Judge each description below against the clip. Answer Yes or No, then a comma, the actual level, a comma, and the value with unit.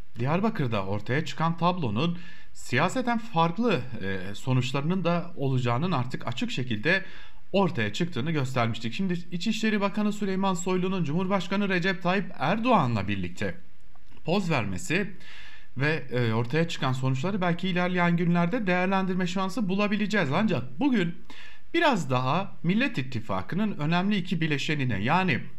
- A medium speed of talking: No, slow, 110 wpm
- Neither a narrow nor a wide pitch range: No, wide, 7.2 semitones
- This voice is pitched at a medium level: Yes, medium, 170 Hz